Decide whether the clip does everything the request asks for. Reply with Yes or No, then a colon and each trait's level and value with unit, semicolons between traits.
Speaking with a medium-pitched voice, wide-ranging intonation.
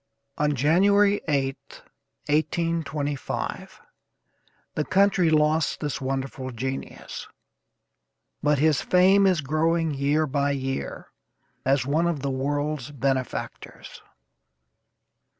No: medium, 150 Hz; average, 3.1 semitones